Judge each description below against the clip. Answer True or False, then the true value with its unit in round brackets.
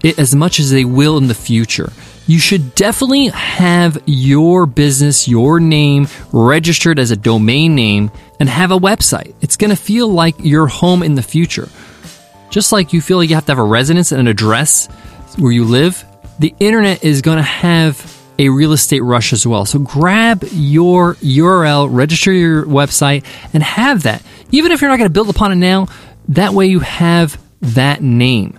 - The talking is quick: False (190 wpm)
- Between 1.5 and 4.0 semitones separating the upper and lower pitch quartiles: False (5.1 semitones)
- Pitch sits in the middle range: True (155 Hz)